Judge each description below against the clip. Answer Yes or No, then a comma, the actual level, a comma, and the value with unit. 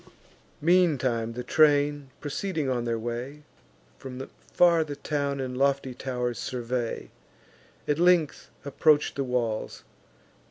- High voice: No, low, 135 Hz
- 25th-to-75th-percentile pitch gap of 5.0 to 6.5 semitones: No, average, 3.2 semitones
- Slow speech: Yes, slow, 115 wpm